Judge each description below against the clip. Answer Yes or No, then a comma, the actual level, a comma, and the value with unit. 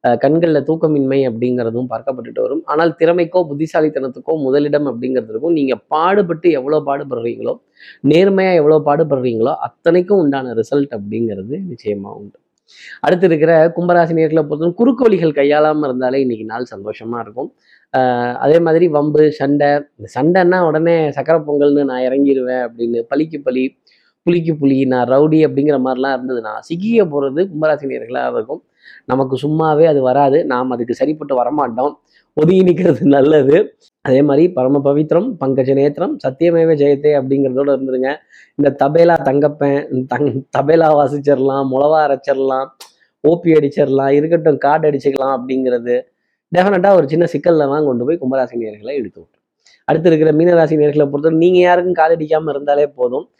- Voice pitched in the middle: Yes, medium, 145 Hz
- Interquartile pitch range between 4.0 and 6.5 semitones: No, average, 3.4 semitones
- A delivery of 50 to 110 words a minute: No, average, 125 wpm